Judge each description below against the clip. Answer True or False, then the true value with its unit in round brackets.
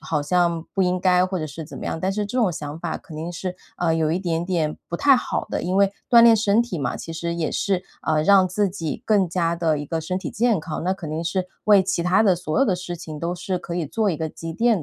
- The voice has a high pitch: False (175 Hz)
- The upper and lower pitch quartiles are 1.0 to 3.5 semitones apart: True (3.0 semitones)